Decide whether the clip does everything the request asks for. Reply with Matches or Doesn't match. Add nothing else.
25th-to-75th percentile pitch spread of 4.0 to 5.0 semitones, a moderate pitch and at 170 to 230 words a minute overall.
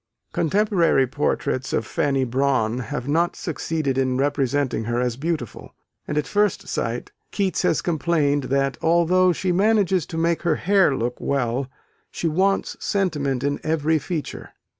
Doesn't match